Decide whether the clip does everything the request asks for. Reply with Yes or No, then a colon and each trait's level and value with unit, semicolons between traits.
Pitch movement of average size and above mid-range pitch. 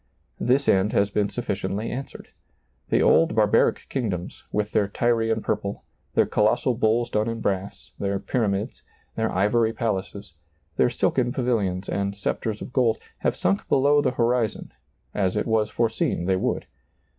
No: average, 3.1 semitones; low, 110 Hz